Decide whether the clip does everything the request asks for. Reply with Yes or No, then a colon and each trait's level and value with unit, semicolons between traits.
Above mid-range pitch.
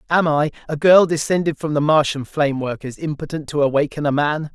No: medium, 150 Hz